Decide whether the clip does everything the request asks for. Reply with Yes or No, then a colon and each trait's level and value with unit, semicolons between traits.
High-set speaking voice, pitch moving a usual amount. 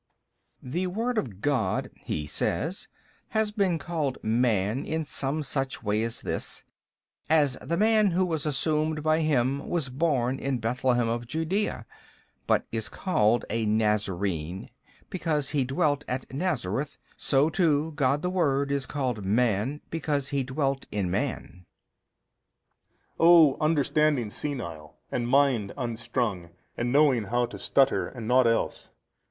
No: low, 135 Hz; average, 4.9 semitones